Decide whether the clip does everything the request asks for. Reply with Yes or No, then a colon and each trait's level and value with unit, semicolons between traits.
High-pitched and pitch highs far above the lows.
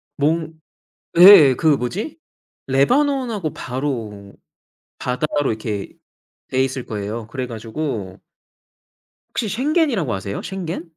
No: medium, 140 Hz; wide, 8.6 semitones